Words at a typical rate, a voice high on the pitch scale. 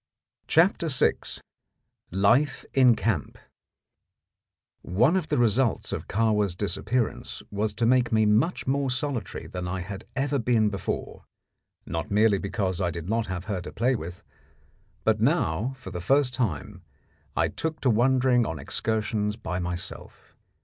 No: average, 145 wpm; low, 110 Hz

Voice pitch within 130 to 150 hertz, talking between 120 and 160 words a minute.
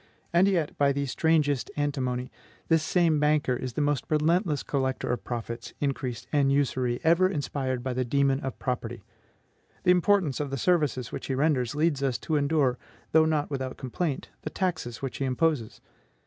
No: medium, 140 Hz; average, 175 wpm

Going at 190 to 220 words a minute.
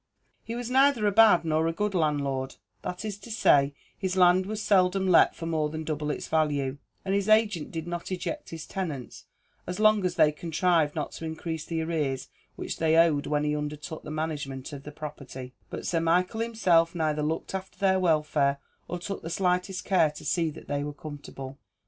Yes: average, 200 wpm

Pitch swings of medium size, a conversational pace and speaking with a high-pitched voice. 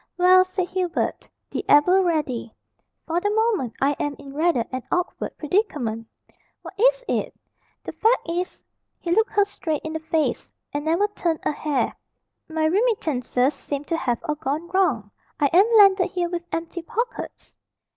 Yes: average, 4.4 semitones; average, 165 wpm; very high, 335 Hz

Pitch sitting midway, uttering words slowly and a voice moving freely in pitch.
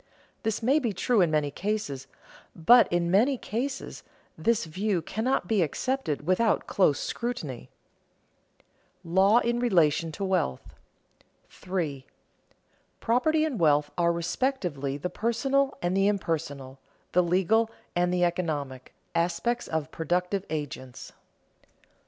Yes: medium, 180 Hz; slow, 120 wpm; wide, 6.5 semitones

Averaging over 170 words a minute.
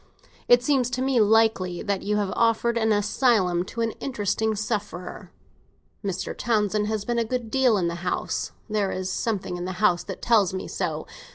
Yes: average, 190 wpm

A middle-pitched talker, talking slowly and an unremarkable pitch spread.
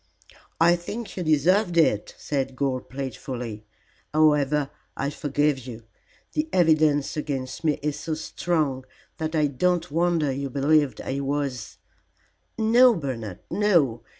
Yes: medium, 150 Hz; slow, 130 wpm; average, 3.7 semitones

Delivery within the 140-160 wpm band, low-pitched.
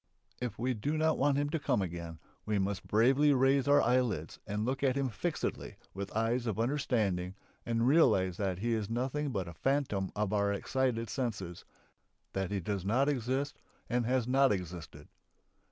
No: average, 175 wpm; low, 115 Hz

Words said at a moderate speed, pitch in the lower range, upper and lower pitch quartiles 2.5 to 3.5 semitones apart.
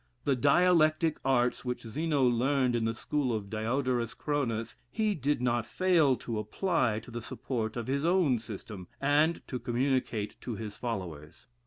No: average, 160 wpm; low, 125 Hz; average, 4.3 semitones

